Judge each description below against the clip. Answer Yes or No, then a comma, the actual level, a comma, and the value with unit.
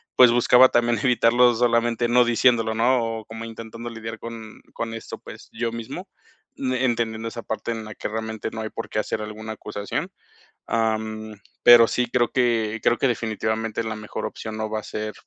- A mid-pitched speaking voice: No, low, 115 Hz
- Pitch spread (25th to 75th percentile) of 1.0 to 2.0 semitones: Yes, narrow, 1.4 semitones